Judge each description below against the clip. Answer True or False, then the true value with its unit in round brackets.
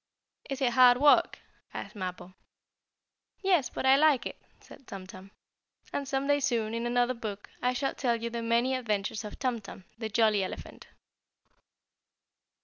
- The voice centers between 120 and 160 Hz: False (240 Hz)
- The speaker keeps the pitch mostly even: False (3.6 semitones)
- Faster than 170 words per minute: False (160 wpm)